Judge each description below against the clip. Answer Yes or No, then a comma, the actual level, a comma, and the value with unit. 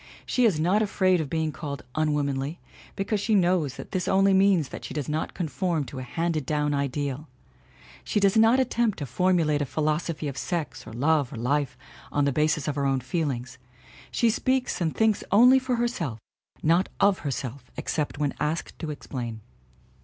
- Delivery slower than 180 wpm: No, average, 185 wpm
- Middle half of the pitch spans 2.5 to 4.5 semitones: No, average, 5.1 semitones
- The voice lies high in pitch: No, medium, 155 Hz